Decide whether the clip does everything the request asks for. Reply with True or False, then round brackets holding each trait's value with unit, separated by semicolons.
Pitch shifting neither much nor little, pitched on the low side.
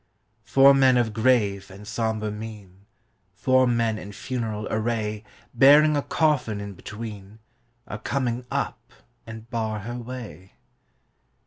True (3.0 semitones; 110 Hz)